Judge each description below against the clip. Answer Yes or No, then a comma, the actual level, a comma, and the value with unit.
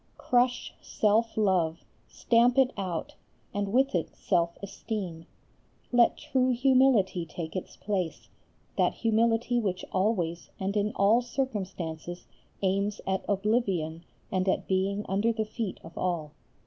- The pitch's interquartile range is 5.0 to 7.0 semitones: No, average, 4.1 semitones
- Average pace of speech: No, slow, 130 wpm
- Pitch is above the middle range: Yes, high, 200 Hz